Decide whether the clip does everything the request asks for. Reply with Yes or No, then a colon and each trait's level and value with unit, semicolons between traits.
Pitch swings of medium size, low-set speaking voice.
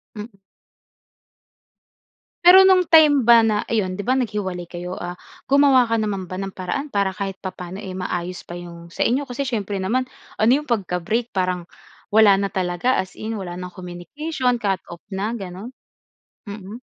No: average, 4.6 semitones; high, 200 Hz